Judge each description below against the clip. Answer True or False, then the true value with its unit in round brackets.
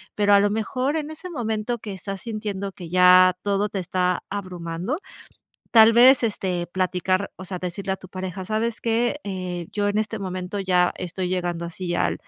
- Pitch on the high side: True (195 Hz)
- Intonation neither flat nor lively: True (3.0 semitones)